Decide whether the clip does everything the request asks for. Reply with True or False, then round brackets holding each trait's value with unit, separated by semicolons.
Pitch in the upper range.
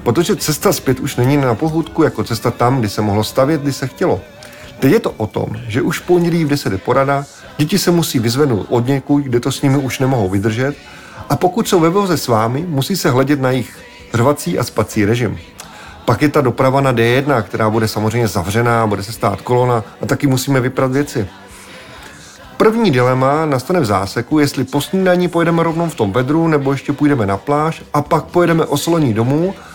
False (135 Hz)